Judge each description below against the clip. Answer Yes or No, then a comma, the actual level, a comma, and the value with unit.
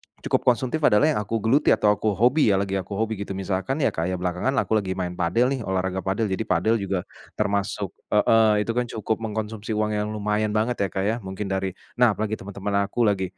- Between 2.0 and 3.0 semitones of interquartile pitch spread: Yes, average, 2.7 semitones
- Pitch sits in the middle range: No, low, 105 Hz